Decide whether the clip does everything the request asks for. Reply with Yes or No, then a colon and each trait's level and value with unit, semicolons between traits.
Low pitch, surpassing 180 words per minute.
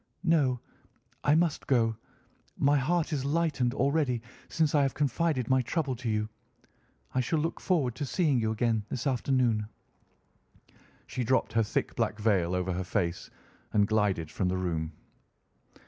No: low, 125 Hz; average, 155 wpm